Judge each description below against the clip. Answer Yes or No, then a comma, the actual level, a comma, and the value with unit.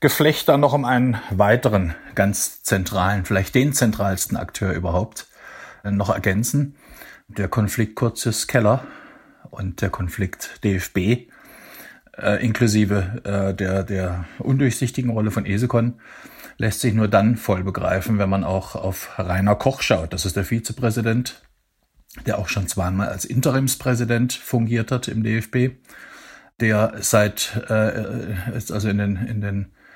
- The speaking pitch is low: Yes, low, 110 Hz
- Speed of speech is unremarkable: Yes, average, 135 wpm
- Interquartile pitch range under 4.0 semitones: Yes, average, 3.4 semitones